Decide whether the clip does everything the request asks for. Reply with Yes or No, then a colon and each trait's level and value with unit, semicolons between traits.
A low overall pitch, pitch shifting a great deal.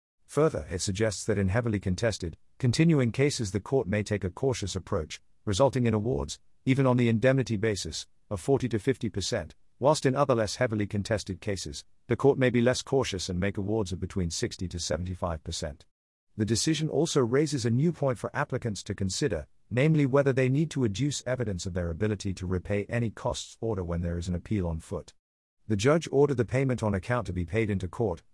Yes: low, 110 Hz; wide, 5.7 semitones